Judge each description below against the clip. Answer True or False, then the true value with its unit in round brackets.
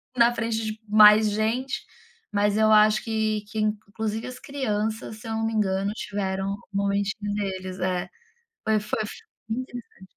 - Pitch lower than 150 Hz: False (215 Hz)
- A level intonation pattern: True (1.5 semitones)